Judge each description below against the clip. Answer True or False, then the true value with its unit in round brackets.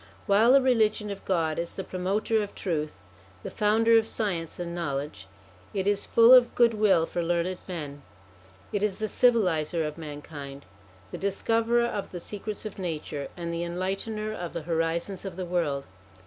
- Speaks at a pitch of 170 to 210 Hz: True (185 Hz)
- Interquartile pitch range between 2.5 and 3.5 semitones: False (4.5 semitones)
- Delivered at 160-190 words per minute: True (170 wpm)